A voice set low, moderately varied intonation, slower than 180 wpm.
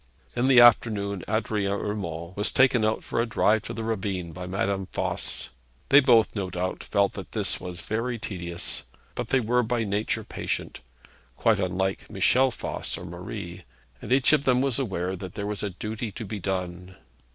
No: low, 105 Hz; average, 4.1 semitones; average, 185 wpm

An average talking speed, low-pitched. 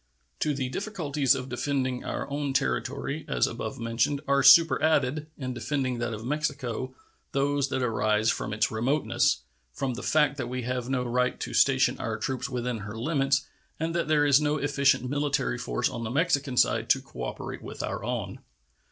Yes: average, 180 wpm; low, 130 Hz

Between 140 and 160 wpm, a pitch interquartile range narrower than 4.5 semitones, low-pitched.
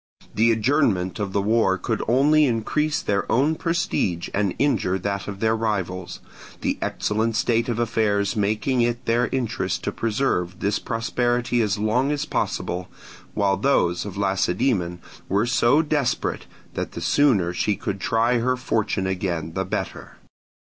Yes: average, 155 wpm; average, 3.9 semitones; low, 110 Hz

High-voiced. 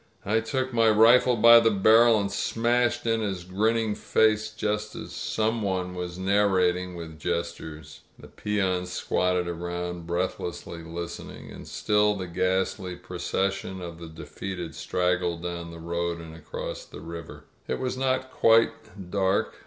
No: very low, 95 Hz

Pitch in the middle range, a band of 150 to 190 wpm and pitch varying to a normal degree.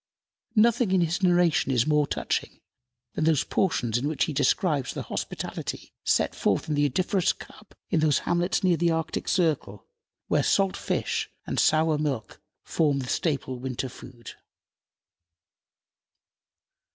No: medium, 155 Hz; average, 140 wpm; average, 4.5 semitones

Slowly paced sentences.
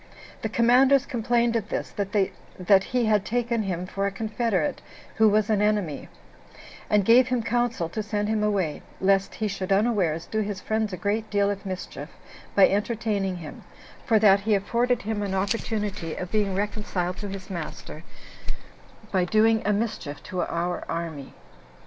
No: average, 165 wpm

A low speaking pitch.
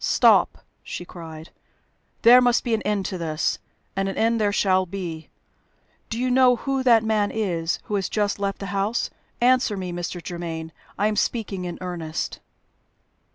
No: high, 200 Hz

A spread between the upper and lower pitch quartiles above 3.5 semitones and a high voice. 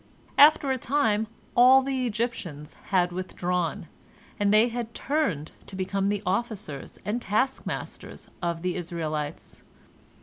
Yes: wide, 5.6 semitones; high, 205 Hz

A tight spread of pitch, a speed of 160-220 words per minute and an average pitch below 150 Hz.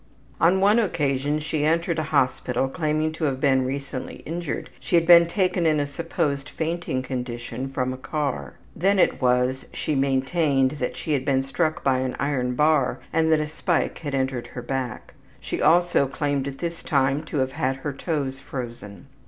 No: average, 3.4 semitones; average, 185 wpm; medium, 140 Hz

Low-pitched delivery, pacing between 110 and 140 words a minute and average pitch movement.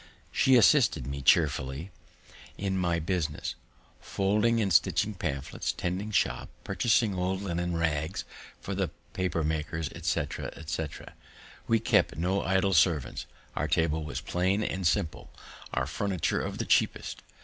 Yes: very low, 90 Hz; slow, 135 wpm; average, 3.8 semitones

